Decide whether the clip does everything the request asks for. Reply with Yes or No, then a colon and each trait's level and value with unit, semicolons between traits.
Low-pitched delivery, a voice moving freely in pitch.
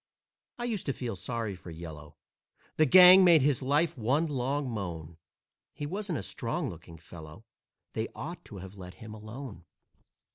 Yes: low, 115 Hz; wide, 8.7 semitones